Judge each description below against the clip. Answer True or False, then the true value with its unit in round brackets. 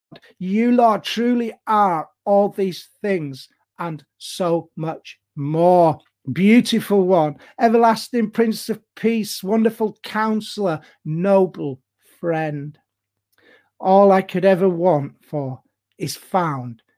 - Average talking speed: False (105 wpm)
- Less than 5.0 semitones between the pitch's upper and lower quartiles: False (5.5 semitones)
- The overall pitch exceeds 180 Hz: True (190 Hz)